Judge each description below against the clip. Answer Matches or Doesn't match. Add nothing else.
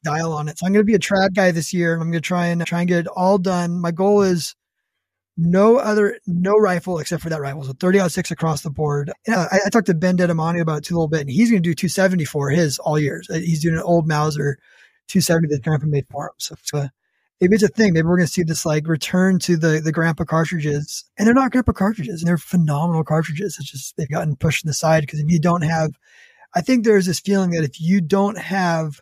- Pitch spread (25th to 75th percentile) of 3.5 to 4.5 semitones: Doesn't match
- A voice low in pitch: Doesn't match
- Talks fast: Matches